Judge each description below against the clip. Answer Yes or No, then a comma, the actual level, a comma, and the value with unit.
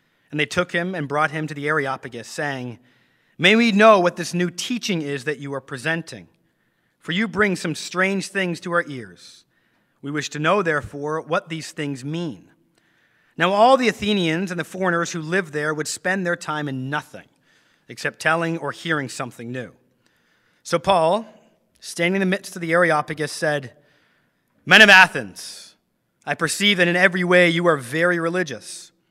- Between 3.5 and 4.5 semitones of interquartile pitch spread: Yes, average, 3.8 semitones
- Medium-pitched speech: Yes, medium, 165 Hz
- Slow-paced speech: No, average, 175 wpm